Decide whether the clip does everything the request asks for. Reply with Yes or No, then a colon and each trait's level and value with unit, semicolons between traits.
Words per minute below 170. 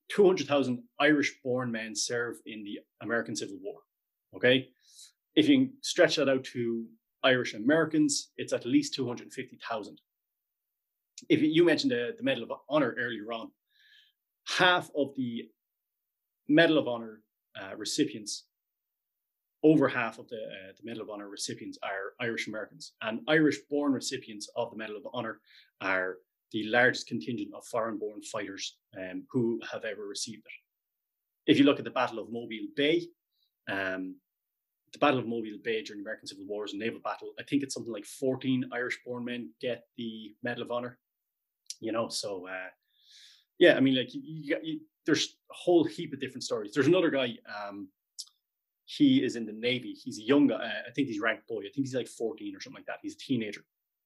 No: average, 180 wpm